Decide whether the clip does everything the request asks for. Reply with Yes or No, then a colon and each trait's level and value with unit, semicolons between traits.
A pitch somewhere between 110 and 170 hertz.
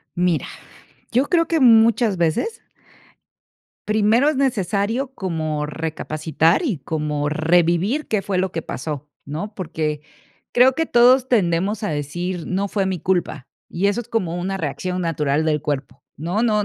No: medium, 185 Hz